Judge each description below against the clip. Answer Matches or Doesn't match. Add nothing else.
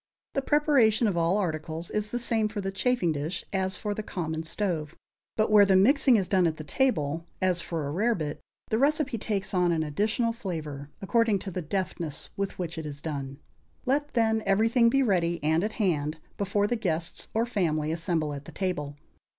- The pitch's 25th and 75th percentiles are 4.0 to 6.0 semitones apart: Matches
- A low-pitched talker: Doesn't match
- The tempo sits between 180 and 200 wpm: Matches